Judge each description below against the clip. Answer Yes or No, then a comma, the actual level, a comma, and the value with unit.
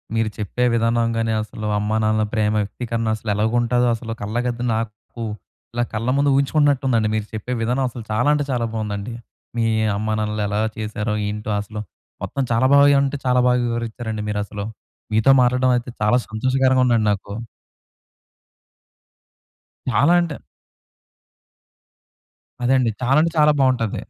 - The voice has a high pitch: No, low, 115 Hz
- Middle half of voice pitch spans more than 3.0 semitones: No, average, 2.7 semitones